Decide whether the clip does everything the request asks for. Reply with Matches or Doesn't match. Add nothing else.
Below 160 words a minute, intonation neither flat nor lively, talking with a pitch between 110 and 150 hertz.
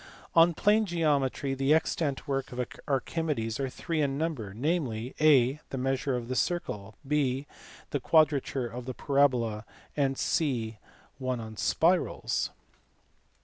Matches